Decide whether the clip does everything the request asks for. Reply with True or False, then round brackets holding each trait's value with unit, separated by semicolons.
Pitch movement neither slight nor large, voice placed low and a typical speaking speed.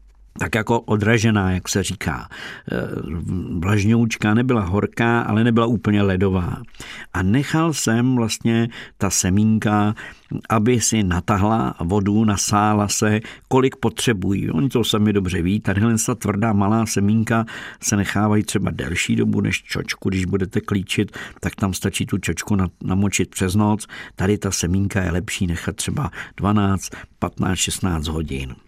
True (3.0 semitones; 105 Hz; 140 wpm)